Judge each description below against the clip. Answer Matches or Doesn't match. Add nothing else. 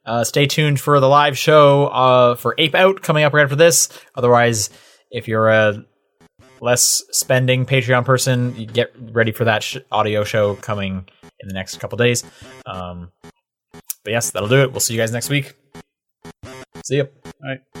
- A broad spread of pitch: Doesn't match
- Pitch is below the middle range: Matches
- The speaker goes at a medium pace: Matches